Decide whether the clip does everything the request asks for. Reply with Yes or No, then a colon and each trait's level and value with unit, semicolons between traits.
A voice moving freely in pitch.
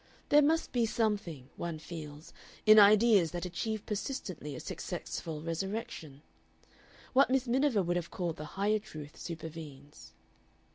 Yes: wide, 5.8 semitones